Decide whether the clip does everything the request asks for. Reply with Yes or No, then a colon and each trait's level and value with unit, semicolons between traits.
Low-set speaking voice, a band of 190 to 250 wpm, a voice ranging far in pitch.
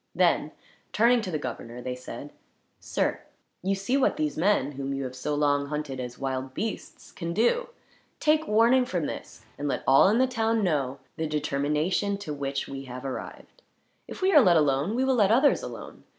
No: medium, 155 Hz; average, 195 wpm; wide, 8.3 semitones